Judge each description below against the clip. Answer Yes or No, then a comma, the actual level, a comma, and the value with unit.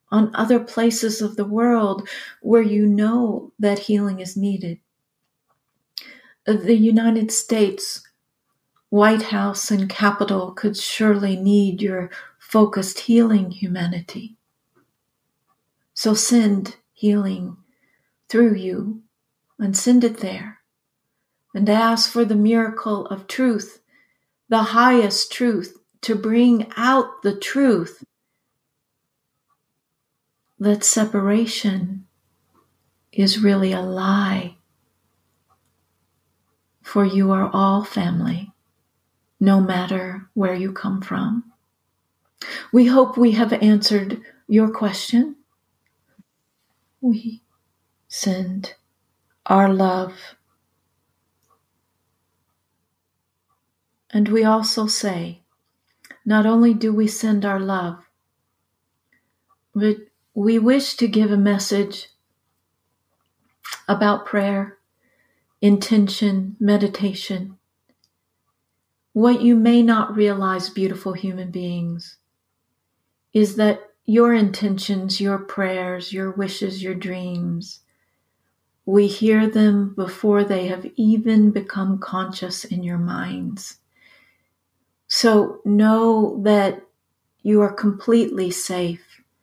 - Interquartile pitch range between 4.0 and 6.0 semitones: No, narrow, 2.6 semitones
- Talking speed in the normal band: No, slow, 95 wpm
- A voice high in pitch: Yes, high, 205 Hz